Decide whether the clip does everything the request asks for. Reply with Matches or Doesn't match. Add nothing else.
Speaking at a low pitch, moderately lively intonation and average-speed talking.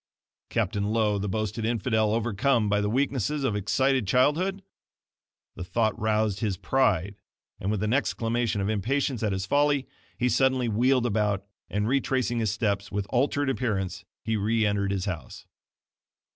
Matches